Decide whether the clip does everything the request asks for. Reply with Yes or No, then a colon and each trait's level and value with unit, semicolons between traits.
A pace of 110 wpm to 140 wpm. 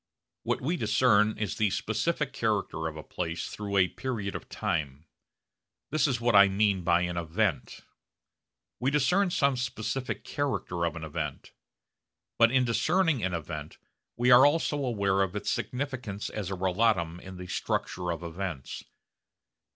No: average, 155 wpm